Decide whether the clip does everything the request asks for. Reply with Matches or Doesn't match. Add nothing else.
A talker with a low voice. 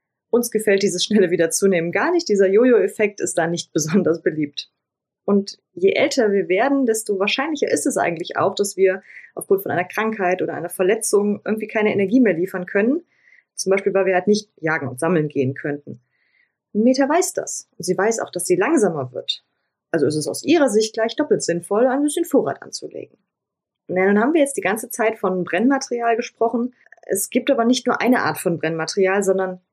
Doesn't match